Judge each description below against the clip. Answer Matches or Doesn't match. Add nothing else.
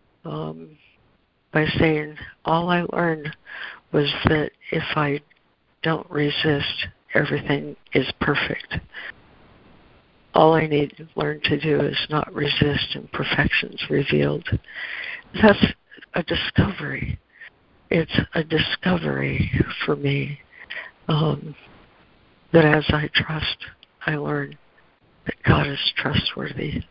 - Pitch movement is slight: Matches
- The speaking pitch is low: Doesn't match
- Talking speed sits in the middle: Doesn't match